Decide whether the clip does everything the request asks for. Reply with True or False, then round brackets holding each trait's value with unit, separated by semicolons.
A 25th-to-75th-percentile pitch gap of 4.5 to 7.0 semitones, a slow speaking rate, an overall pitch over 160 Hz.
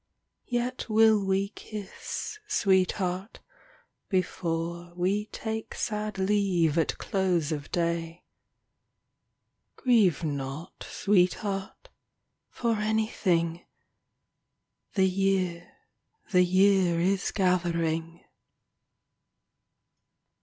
False (3.4 semitones; 75 wpm; 185 Hz)